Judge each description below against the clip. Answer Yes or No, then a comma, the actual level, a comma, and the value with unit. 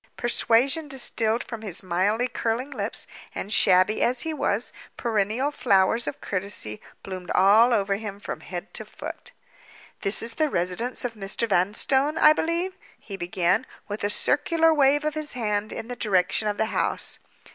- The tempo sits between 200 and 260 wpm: No, average, 165 wpm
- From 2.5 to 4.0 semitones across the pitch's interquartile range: No, average, 4.8 semitones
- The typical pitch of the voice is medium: No, high, 220 Hz